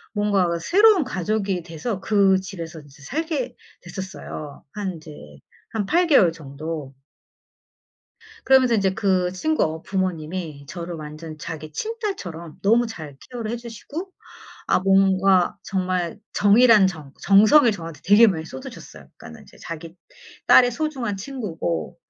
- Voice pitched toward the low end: No, high, 190 Hz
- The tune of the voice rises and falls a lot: Yes, wide, 5.7 semitones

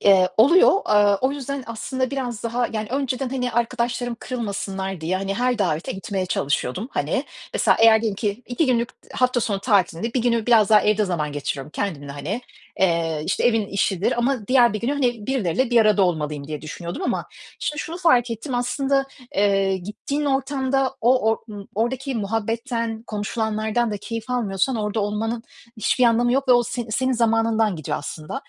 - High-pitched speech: Yes, high, 225 Hz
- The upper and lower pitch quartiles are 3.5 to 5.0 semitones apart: Yes, average, 4.0 semitones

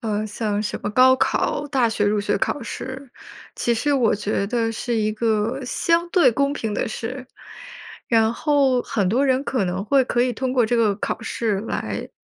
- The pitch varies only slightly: No, average, 3.4 semitones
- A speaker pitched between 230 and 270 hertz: Yes, high, 235 Hz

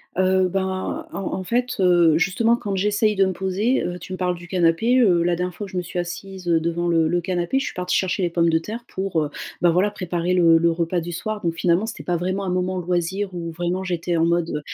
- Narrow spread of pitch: Yes, narrow, 1.9 semitones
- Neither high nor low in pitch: Yes, medium, 180 Hz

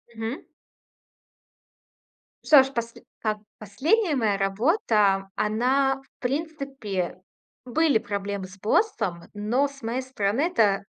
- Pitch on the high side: Yes, high, 230 Hz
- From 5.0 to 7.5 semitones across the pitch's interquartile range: Yes, wide, 5.4 semitones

